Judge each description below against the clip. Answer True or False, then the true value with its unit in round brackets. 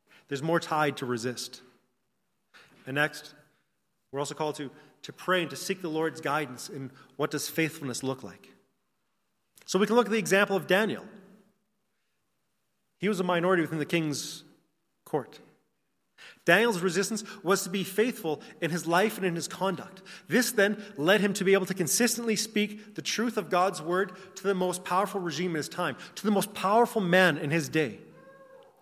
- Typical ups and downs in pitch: True (5.0 semitones)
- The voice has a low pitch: False (185 Hz)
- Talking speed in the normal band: True (180 wpm)